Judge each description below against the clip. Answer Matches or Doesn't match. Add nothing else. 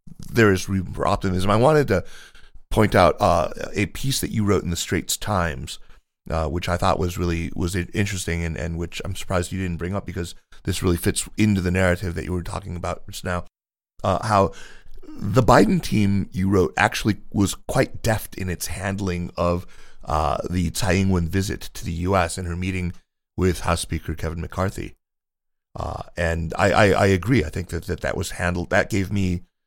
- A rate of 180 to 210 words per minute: Matches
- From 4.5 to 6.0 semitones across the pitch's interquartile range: Doesn't match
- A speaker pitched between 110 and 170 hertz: Doesn't match